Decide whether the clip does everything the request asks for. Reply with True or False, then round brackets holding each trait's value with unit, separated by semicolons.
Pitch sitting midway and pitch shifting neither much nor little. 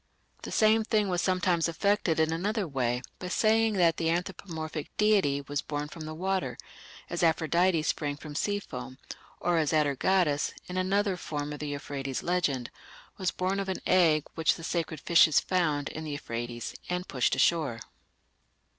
True (165 Hz; 4.1 semitones)